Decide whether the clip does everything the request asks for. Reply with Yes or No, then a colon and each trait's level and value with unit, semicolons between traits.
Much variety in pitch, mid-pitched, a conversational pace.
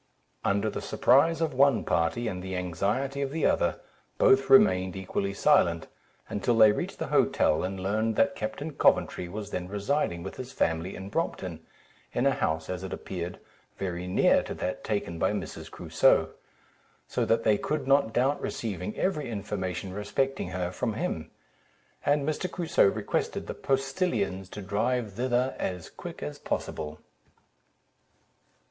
No: wide, 6.4 semitones; low, 105 Hz; average, 155 wpm